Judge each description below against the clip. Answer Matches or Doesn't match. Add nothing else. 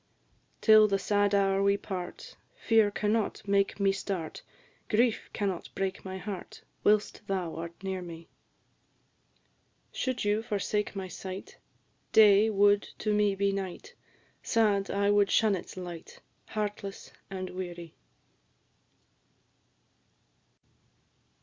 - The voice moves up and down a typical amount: Doesn't match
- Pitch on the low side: Doesn't match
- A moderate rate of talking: Doesn't match